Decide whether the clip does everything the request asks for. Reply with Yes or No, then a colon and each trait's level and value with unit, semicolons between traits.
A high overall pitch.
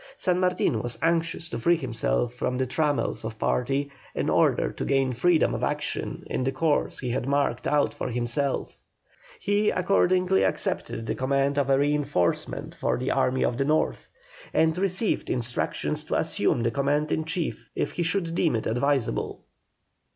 No: medium, 140 Hz